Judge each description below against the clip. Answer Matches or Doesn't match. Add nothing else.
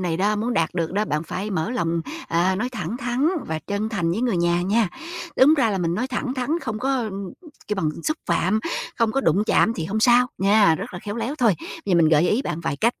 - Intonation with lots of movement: Matches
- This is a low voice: Doesn't match